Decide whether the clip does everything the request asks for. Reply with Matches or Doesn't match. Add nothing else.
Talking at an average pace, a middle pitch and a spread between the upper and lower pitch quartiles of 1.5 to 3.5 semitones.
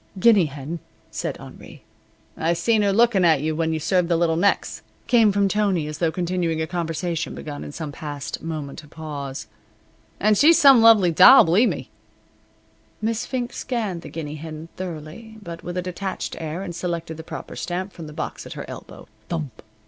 Doesn't match